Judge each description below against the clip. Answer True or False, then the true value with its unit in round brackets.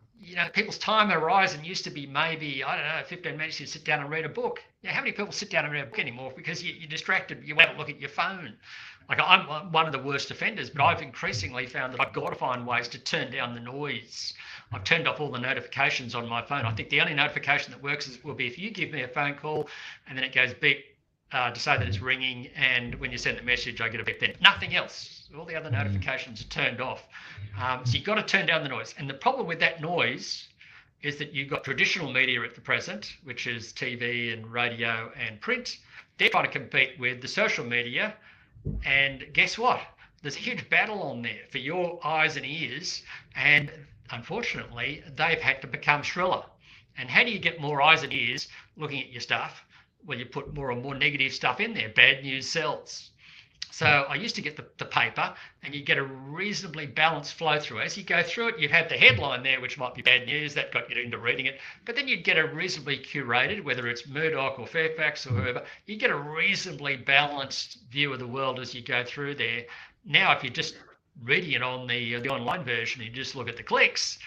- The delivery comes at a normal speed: False (235 wpm)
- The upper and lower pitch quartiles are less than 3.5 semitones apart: False (4.0 semitones)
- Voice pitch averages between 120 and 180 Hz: True (140 Hz)